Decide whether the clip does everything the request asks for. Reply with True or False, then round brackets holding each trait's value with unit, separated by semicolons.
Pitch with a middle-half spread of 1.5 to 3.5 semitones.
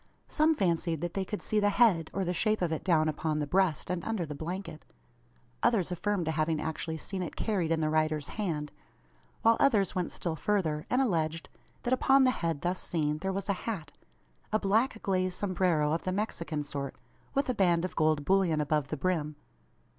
False (4.2 semitones)